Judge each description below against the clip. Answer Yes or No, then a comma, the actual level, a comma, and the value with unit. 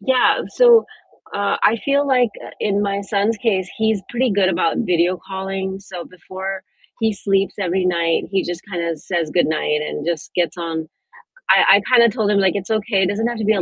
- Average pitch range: Yes, average, 3.5 semitones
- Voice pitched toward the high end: Yes, high, 195 Hz